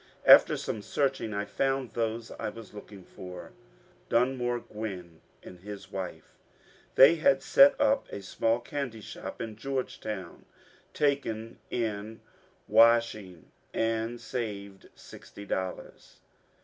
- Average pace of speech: No, slow, 120 wpm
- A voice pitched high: No, low, 110 Hz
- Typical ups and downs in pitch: Yes, average, 3.4 semitones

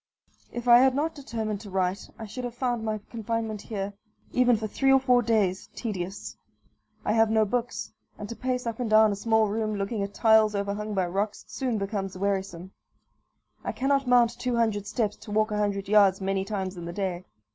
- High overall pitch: Yes, high, 215 Hz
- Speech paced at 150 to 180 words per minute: No, average, 200 wpm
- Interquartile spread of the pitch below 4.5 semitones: Yes, average, 3.0 semitones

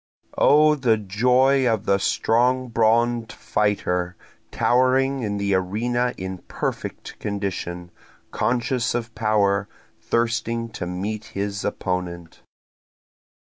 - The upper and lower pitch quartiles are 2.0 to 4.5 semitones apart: Yes, average, 3.7 semitones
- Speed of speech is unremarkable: No, slow, 100 wpm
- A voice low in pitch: Yes, low, 110 Hz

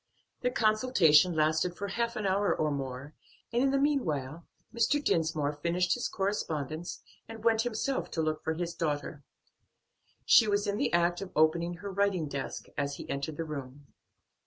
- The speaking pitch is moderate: Yes, medium, 170 Hz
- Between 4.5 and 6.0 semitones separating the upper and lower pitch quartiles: Yes, wide, 5.5 semitones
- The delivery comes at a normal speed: Yes, average, 170 wpm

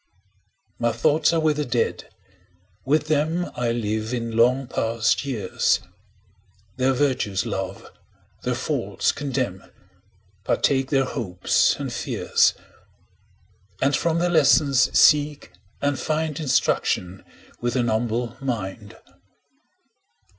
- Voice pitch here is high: No, low, 130 Hz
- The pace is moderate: No, slow, 110 wpm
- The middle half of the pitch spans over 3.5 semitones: Yes, average, 4.4 semitones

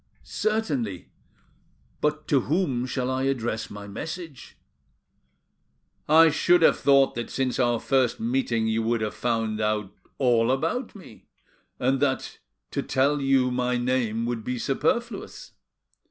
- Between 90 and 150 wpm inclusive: Yes, slow, 135 wpm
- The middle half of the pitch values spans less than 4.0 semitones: Yes, average, 3.6 semitones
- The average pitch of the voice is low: Yes, low, 130 Hz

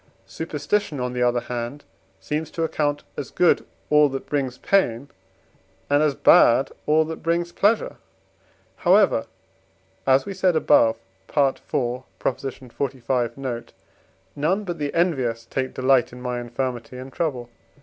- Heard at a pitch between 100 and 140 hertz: Yes, low, 135 Hz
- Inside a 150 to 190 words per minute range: No, slow, 135 wpm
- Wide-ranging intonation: No, average, 4.2 semitones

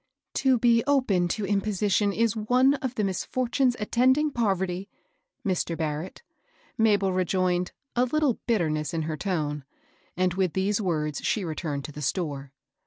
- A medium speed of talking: Yes, average, 160 wpm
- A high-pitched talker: Yes, high, 195 Hz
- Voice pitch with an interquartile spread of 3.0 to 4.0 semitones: No, wide, 5.4 semitones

